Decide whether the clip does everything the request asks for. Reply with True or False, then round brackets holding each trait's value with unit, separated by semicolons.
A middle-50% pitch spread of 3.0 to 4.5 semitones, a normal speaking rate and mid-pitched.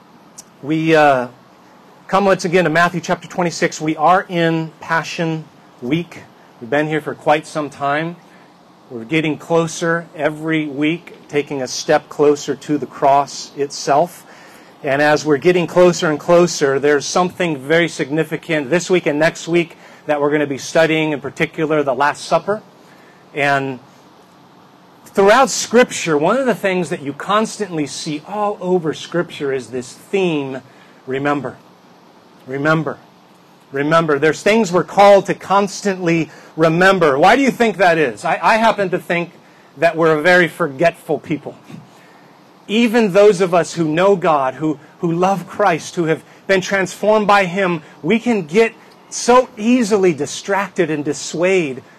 True (4.1 semitones; 150 wpm; 165 Hz)